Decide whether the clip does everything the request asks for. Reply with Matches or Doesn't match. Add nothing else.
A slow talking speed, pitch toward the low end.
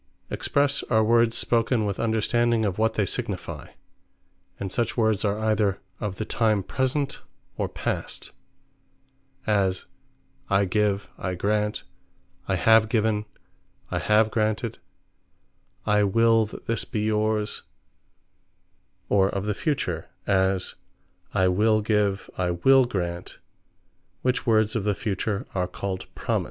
Matches